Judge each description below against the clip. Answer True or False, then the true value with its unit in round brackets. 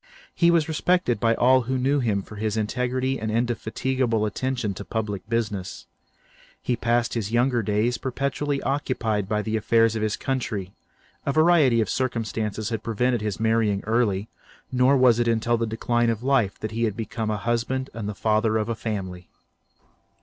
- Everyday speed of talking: True (170 wpm)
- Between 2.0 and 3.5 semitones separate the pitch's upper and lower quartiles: True (2.9 semitones)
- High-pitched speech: False (115 Hz)